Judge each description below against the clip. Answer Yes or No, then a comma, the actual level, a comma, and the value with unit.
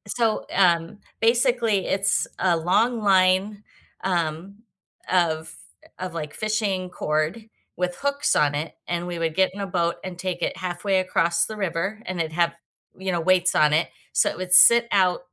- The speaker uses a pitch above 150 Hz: Yes, medium, 185 Hz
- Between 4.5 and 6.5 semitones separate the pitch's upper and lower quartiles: No, average, 3.1 semitones